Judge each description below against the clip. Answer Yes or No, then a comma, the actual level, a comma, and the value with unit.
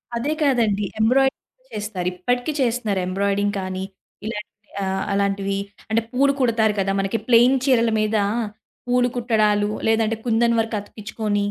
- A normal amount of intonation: Yes, average, 3.1 semitones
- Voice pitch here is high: Yes, high, 220 Hz